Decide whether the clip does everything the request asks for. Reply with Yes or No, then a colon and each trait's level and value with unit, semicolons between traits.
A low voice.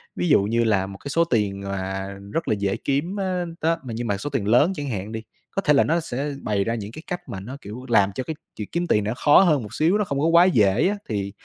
Yes: low, 120 Hz